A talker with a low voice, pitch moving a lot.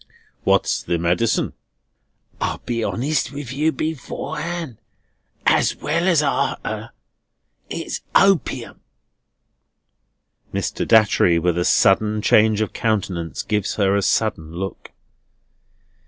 Yes: low, 110 Hz; wide, 7.3 semitones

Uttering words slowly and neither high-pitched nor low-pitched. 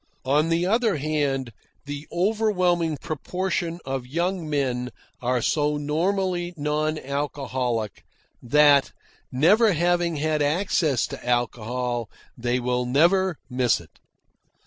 Yes: slow, 110 wpm; medium, 150 Hz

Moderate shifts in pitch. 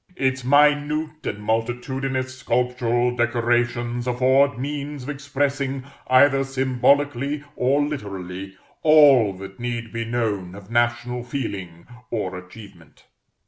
Yes: average, 3.1 semitones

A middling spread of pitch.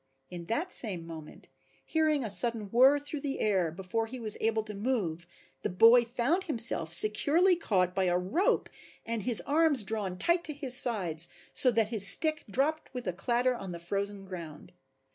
No: wide, 6.2 semitones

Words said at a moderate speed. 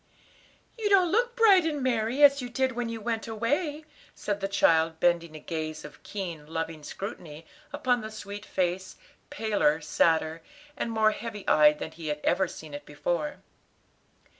Yes: average, 165 wpm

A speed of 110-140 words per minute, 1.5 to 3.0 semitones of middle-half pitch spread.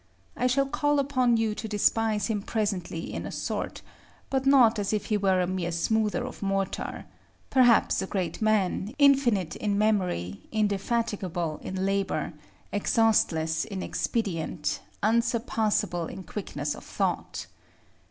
No: slow, 135 wpm; average, 3.6 semitones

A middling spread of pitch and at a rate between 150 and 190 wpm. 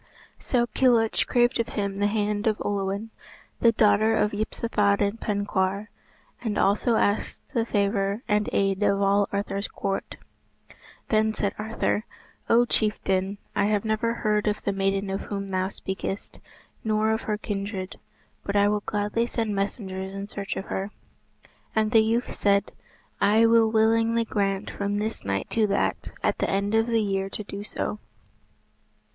No: narrow, 1.8 semitones; average, 160 wpm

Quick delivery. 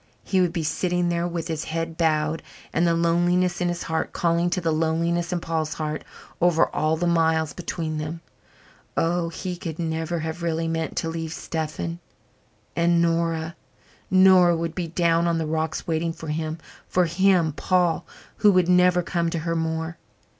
No: average, 175 wpm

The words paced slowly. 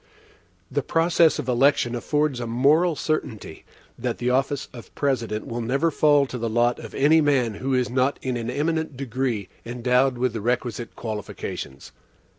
No: average, 165 wpm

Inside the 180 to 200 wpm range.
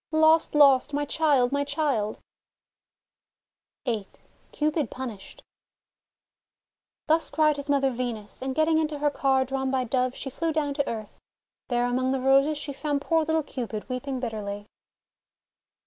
No: average, 145 wpm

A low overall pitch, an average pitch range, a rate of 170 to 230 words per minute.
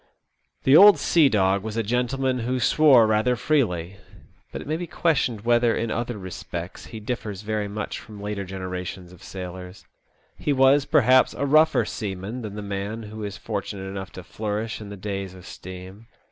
Yes: low, 105 Hz; average, 4.3 semitones; average, 180 wpm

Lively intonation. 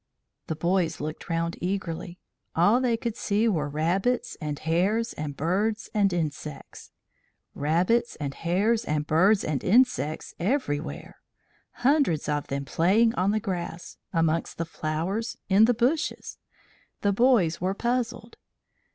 Yes: wide, 6.0 semitones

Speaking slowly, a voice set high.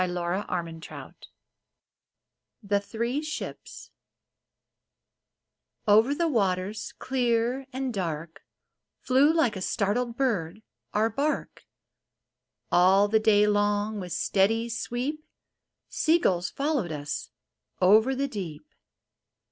Yes: slow, 100 wpm; high, 215 Hz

